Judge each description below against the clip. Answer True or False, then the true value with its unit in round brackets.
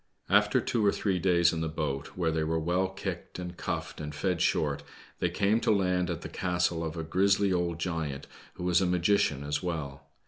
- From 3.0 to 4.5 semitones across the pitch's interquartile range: False (2.5 semitones)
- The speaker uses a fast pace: True (210 wpm)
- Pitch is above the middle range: False (85 Hz)